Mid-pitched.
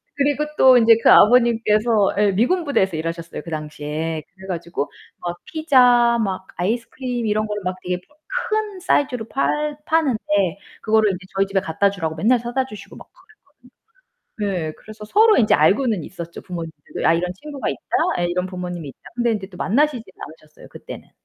No: high, 210 Hz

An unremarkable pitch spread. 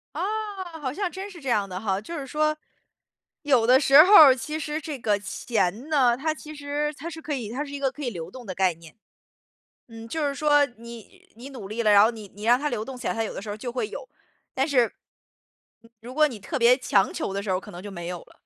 No: wide, 5.9 semitones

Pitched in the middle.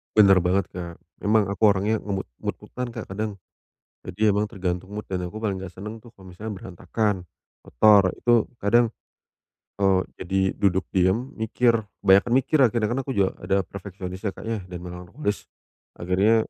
No: low, 100 Hz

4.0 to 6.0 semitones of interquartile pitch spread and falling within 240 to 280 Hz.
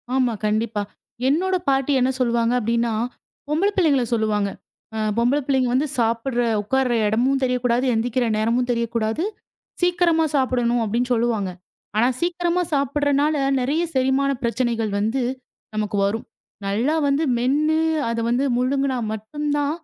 No: average, 3.4 semitones; very high, 250 Hz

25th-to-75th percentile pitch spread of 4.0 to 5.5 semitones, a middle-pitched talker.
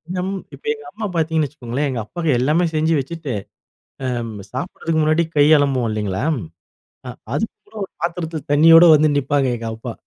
Yes: average, 4.4 semitones; medium, 150 Hz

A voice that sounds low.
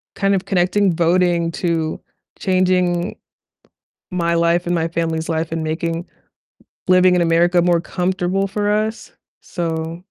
No: medium, 175 Hz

